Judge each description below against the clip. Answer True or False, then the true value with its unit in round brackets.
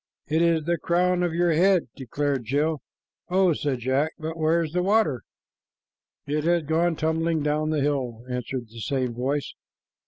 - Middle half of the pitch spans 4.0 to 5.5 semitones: False (3.6 semitones)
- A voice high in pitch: False (155 Hz)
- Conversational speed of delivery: True (160 wpm)